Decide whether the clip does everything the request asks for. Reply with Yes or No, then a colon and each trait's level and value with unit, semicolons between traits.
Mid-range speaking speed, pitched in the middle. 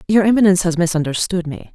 Yes: average, 170 wpm; medium, 180 Hz